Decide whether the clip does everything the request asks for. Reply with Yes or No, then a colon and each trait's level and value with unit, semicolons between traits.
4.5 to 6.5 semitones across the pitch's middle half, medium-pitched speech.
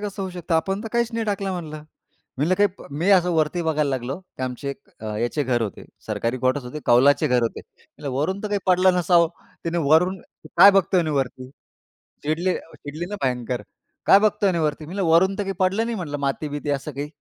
Yes: average, 5.2 semitones; medium, 160 Hz